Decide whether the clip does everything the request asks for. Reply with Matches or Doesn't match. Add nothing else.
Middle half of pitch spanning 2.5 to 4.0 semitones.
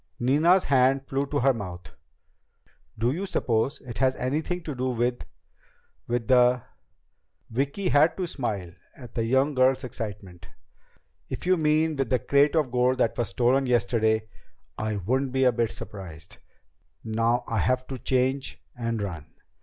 Matches